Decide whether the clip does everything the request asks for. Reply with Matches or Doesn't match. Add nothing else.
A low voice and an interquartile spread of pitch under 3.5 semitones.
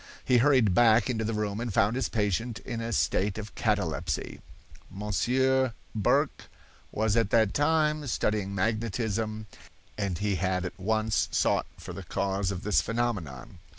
Matches